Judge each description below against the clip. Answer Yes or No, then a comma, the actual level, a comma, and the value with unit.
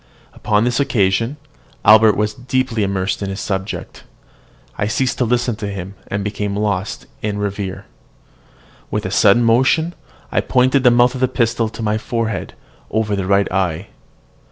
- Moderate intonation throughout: Yes, average, 3.3 semitones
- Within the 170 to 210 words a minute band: No, average, 160 wpm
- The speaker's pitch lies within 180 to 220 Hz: No, low, 110 Hz